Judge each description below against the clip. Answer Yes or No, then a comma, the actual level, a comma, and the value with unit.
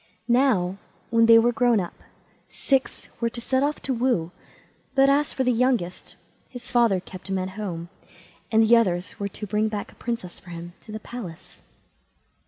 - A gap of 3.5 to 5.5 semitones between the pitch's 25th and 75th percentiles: Yes, average, 4.7 semitones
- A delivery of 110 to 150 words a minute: No, average, 185 wpm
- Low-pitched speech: No, high, 220 Hz